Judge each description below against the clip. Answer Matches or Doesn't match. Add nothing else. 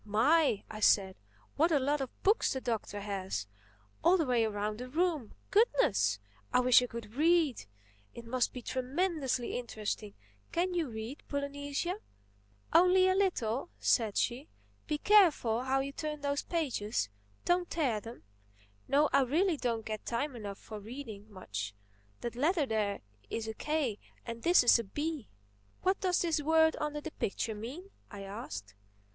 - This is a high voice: Matches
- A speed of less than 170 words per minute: Matches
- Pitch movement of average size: Doesn't match